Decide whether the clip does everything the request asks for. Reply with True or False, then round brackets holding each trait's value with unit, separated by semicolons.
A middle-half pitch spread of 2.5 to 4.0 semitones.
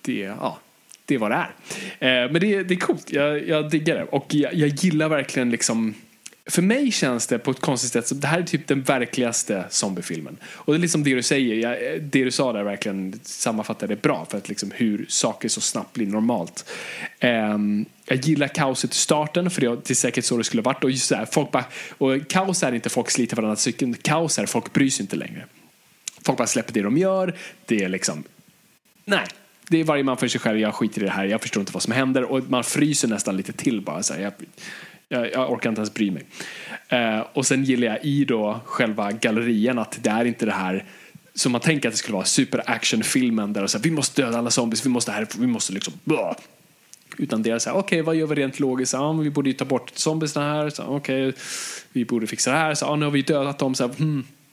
False (4.4 semitones)